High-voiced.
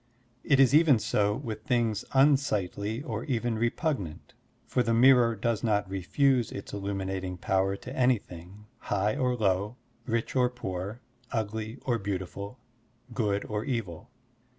No: low, 110 Hz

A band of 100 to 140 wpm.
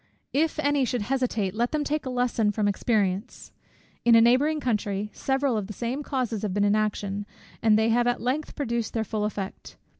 No: average, 200 wpm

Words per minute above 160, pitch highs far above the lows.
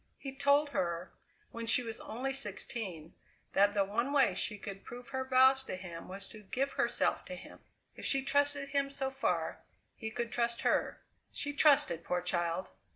Yes: average, 180 wpm; wide, 5.9 semitones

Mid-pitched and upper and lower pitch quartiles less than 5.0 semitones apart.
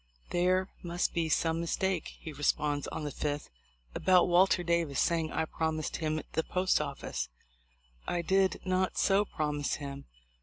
Yes: medium, 165 Hz; average, 3.4 semitones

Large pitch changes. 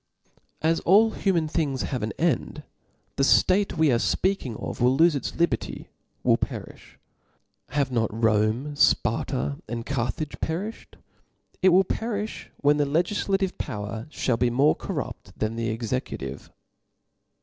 Yes: wide, 6.9 semitones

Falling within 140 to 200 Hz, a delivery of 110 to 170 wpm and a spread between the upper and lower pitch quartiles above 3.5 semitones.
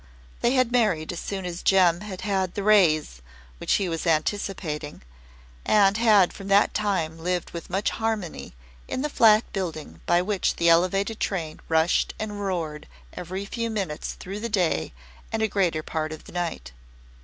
Yes: medium, 185 Hz; average, 165 wpm; average, 4.0 semitones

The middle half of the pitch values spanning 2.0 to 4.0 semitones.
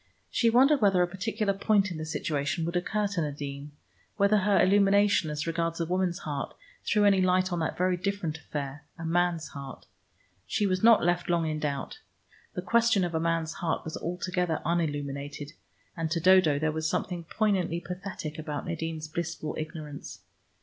Yes: average, 3.5 semitones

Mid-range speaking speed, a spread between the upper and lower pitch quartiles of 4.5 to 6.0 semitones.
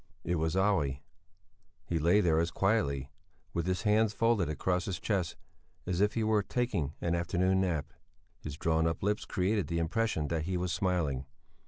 No: average, 175 wpm; average, 3.8 semitones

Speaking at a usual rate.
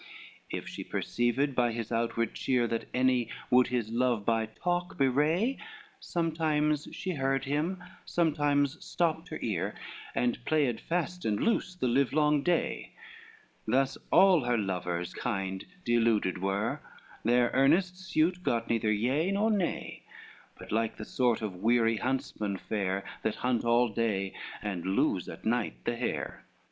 Yes: average, 145 wpm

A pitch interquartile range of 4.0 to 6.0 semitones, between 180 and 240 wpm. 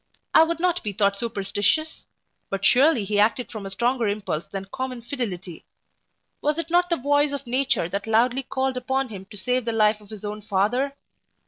Yes: average, 4.9 semitones; average, 195 wpm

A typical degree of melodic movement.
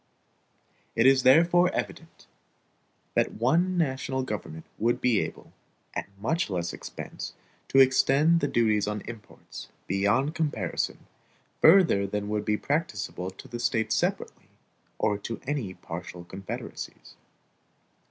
No: wide, 6.0 semitones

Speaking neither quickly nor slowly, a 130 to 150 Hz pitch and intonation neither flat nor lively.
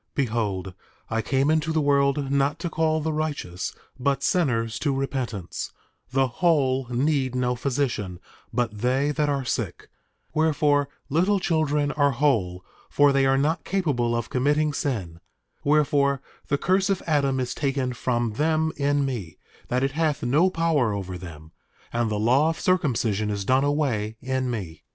Yes: average, 160 wpm; low, 135 Hz; average, 4.1 semitones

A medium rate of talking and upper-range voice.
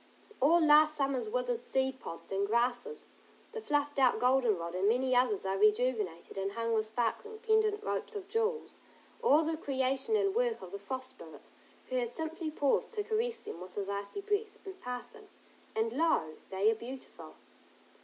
Yes: average, 175 wpm; very high, 265 Hz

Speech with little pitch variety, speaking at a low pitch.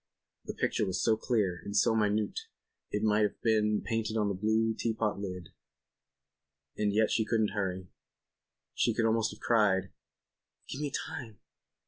Yes: narrow, 1.8 semitones; low, 110 Hz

